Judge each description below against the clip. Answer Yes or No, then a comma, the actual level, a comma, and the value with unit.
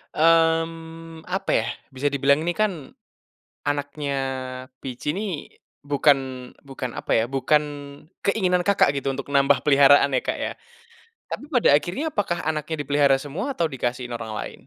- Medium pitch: Yes, medium, 145 Hz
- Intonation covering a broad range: No, average, 3.3 semitones